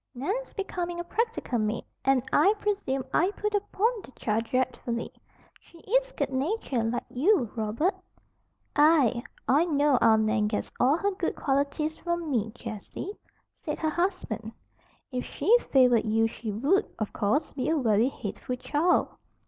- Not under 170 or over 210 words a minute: No, average, 155 wpm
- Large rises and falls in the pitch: Yes, wide, 7.2 semitones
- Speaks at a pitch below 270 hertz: No, very high, 275 Hz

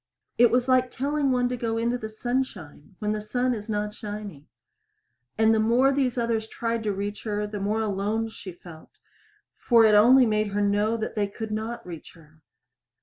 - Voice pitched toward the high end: Yes, high, 220 Hz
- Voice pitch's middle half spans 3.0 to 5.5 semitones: No, narrow, 2.6 semitones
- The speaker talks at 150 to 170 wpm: No, average, 190 wpm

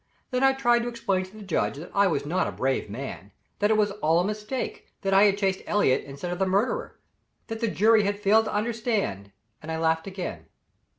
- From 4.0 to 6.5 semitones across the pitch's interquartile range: Yes, average, 4.8 semitones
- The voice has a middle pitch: No, high, 200 Hz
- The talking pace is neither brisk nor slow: No, fast, 225 wpm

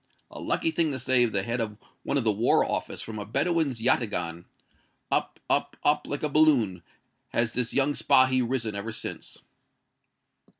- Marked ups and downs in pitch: No, average, 4.4 semitones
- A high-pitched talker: No, low, 120 Hz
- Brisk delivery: No, average, 170 wpm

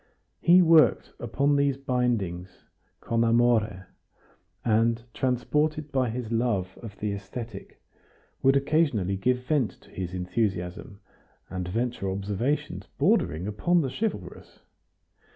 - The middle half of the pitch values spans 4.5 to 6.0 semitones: Yes, wide, 5.5 semitones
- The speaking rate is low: Yes, slow, 115 wpm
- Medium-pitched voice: No, low, 115 Hz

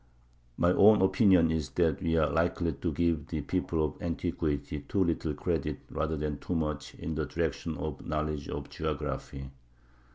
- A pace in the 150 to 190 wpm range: Yes, average, 170 wpm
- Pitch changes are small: Yes, narrow, 2.2 semitones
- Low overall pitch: Yes, very low, 80 Hz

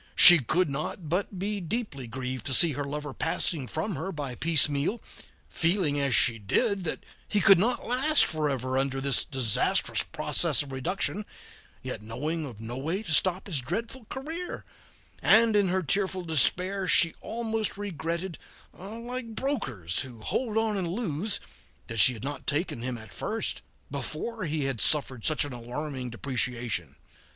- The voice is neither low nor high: Yes, medium, 155 Hz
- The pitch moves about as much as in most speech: No, wide, 7.1 semitones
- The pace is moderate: Yes, average, 160 wpm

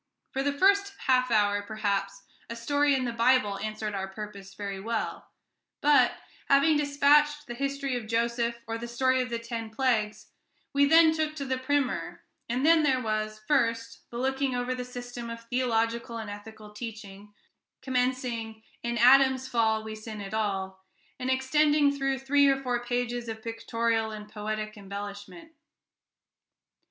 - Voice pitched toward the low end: No, high, 235 Hz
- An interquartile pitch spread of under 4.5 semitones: Yes, average, 3.6 semitones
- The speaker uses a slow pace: No, average, 155 wpm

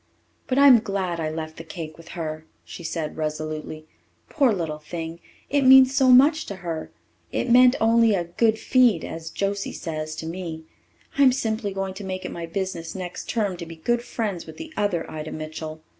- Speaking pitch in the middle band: Yes, medium, 180 Hz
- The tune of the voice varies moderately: No, wide, 6.1 semitones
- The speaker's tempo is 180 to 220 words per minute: Yes, average, 190 wpm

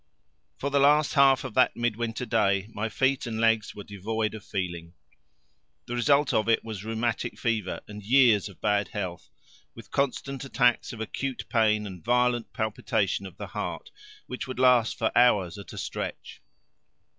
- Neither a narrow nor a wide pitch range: Yes, average, 3.2 semitones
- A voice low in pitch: Yes, low, 115 Hz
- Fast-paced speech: No, average, 170 wpm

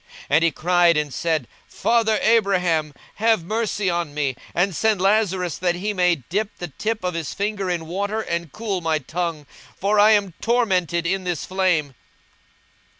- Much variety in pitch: No, average, 3.8 semitones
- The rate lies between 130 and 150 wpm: No, average, 170 wpm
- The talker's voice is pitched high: No, medium, 180 Hz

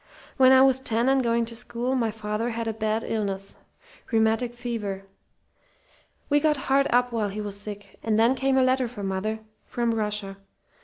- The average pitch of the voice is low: No, high, 230 Hz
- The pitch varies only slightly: No, average, 3.0 semitones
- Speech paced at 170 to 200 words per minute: Yes, average, 185 wpm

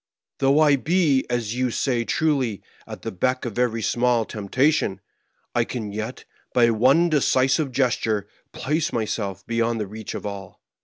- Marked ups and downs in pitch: No, average, 3.8 semitones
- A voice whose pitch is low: Yes, low, 120 Hz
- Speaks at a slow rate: No, average, 155 wpm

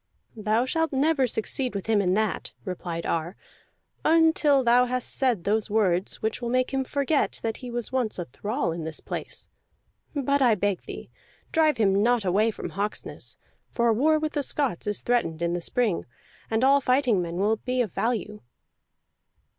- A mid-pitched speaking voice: No, high, 230 Hz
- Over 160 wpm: Yes, average, 180 wpm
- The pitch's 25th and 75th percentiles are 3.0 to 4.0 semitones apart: No, average, 4.7 semitones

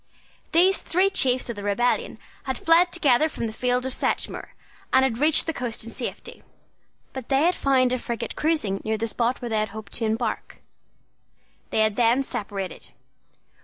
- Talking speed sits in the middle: Yes, average, 180 wpm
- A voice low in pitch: No, high, 245 Hz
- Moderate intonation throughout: Yes, average, 4.0 semitones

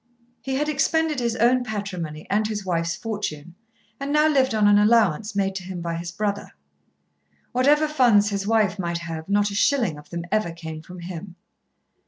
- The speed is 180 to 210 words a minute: Yes, average, 185 wpm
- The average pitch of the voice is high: Yes, high, 205 Hz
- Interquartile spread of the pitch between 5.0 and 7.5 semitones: Yes, wide, 5.5 semitones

